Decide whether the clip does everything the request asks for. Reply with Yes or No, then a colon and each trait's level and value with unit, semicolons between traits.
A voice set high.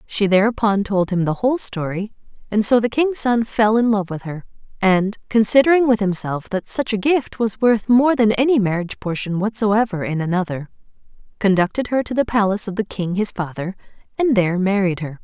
Yes: high, 210 Hz